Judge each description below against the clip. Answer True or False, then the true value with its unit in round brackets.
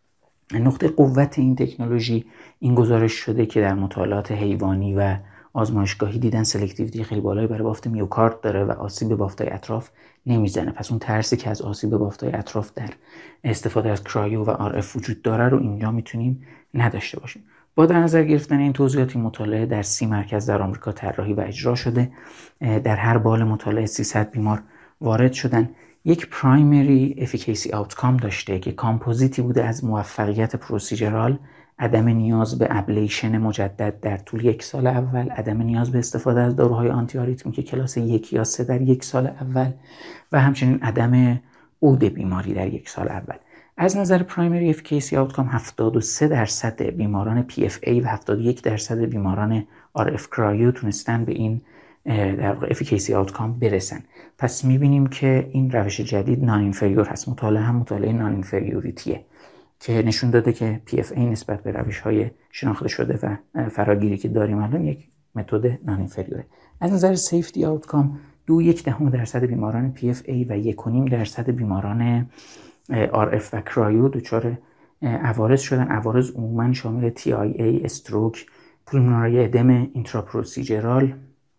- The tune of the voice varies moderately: True (3.0 semitones)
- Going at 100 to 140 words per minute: False (150 wpm)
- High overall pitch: False (115 Hz)